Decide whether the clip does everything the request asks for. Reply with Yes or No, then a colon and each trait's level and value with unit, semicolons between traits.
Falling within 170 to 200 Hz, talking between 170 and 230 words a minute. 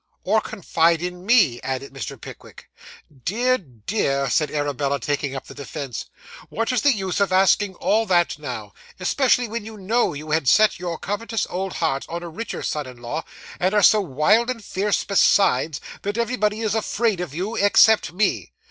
Yes: medium, 185 Hz; average, 180 wpm